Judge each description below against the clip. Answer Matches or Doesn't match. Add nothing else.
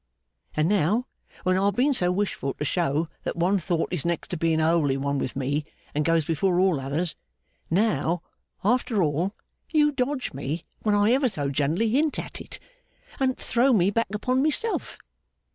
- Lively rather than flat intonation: Matches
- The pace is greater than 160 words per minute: Matches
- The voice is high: Doesn't match